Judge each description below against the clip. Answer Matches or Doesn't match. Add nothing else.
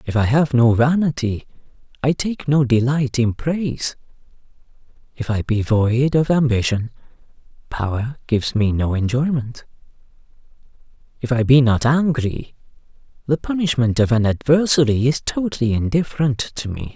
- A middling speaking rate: Doesn't match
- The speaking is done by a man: Matches